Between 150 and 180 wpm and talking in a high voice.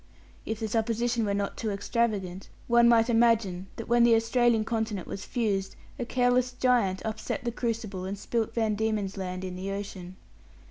Yes: average, 175 wpm; high, 220 Hz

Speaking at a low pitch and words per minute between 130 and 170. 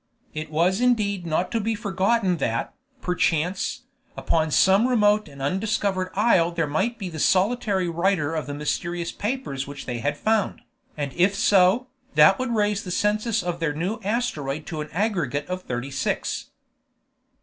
No: medium, 185 Hz; average, 160 wpm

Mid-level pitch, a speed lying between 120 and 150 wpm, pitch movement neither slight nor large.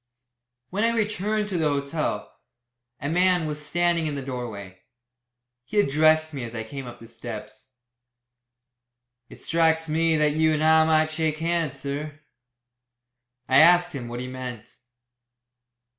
Yes: medium, 155 Hz; average, 145 wpm; average, 4.1 semitones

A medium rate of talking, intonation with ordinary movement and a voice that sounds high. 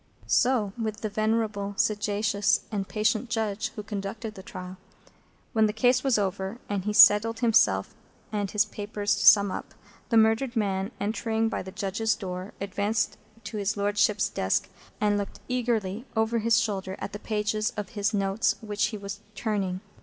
No: average, 170 wpm; narrow, 1.7 semitones; high, 210 Hz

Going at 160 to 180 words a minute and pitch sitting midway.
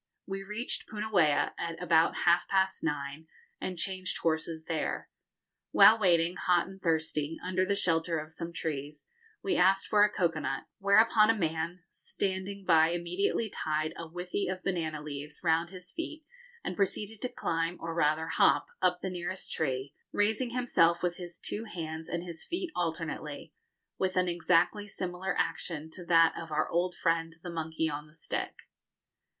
Yes: average, 165 wpm; medium, 175 Hz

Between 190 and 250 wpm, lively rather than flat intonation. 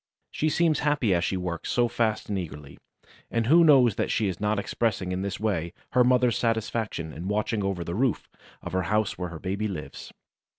No: fast, 205 wpm; average, 4.6 semitones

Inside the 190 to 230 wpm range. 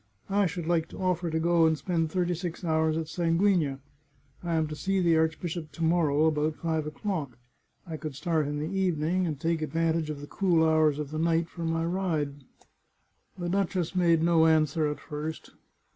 Yes: average, 195 wpm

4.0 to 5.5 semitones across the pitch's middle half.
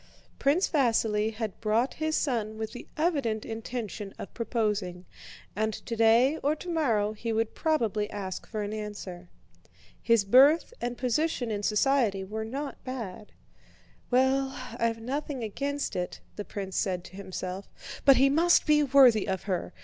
Yes: average, 4.5 semitones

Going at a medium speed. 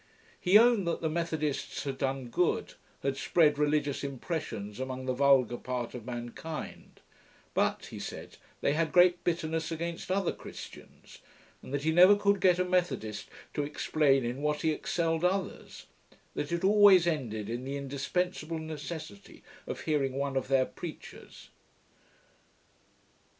Yes: average, 145 wpm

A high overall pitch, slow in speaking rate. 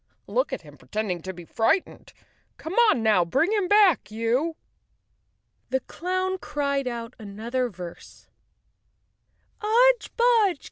Yes: very high, 265 Hz; slow, 130 wpm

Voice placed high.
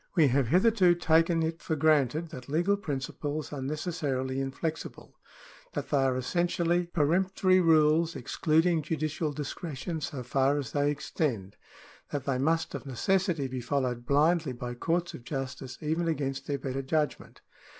No: medium, 150 Hz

